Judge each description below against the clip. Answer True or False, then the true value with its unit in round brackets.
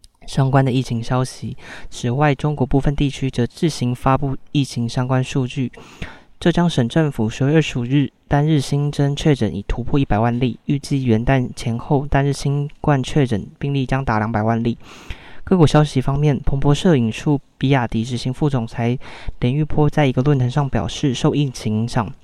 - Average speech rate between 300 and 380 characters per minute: False (285 characters per minute)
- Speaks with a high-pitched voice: False (135 Hz)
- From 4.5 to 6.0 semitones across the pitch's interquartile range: False (3.1 semitones)